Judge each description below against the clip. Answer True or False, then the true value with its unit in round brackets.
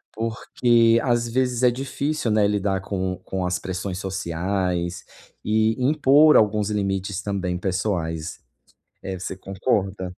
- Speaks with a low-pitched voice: True (100 Hz)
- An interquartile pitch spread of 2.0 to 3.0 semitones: False (3.7 semitones)